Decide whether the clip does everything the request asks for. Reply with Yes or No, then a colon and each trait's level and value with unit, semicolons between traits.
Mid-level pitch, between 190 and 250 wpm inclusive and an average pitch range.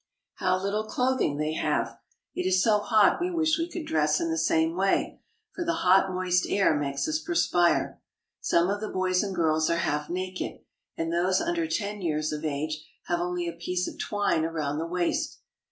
Yes: medium, 180 Hz; average, 195 wpm; average, 4.1 semitones